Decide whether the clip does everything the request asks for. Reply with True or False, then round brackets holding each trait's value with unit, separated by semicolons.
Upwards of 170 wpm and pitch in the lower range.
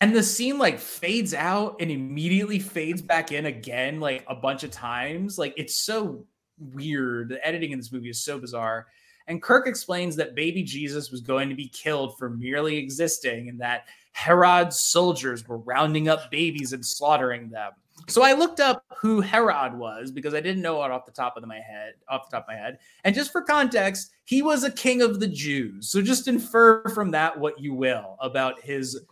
False (205 wpm; 155 Hz)